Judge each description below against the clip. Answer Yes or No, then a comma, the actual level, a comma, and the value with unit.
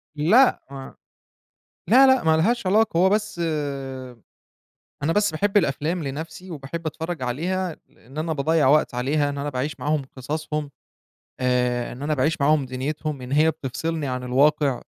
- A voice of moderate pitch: Yes, medium, 155 Hz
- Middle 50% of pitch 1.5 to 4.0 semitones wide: Yes, average, 3.6 semitones